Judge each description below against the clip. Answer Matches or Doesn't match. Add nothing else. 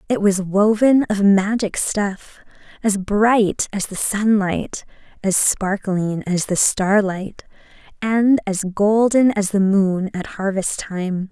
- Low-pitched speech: Doesn't match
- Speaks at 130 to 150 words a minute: Matches